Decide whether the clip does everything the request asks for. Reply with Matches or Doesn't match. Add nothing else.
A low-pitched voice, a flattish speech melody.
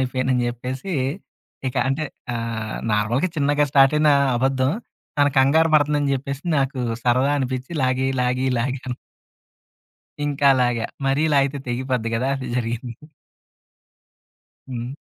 Matches